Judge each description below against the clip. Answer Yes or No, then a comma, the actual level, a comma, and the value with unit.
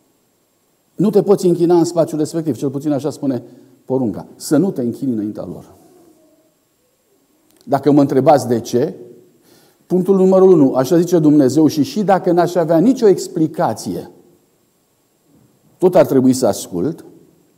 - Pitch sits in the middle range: Yes, medium, 170 Hz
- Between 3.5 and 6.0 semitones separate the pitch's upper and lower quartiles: Yes, average, 4.8 semitones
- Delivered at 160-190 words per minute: No, average, 140 wpm